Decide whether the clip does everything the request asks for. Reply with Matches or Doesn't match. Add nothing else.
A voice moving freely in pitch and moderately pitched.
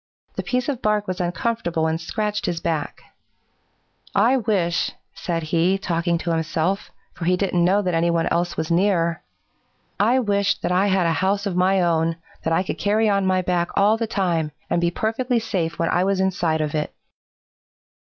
Doesn't match